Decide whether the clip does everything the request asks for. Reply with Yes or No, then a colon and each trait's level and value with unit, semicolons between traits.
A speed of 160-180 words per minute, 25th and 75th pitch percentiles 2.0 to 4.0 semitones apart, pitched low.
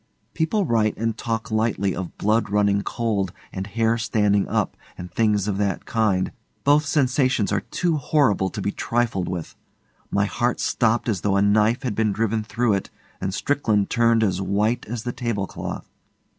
Yes: average, 170 wpm; average, 2.8 semitones; low, 110 Hz